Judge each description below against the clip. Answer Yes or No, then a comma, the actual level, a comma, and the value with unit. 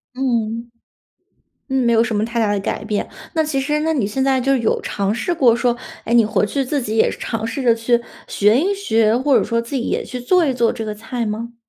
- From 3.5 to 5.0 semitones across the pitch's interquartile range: No, average, 3.1 semitones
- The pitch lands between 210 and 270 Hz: Yes, high, 235 Hz